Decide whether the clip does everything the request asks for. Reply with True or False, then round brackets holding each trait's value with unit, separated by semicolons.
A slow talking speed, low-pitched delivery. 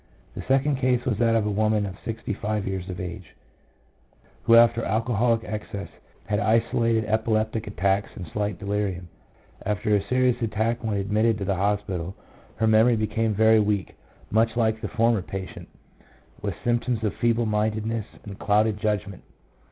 False (160 wpm; 110 Hz)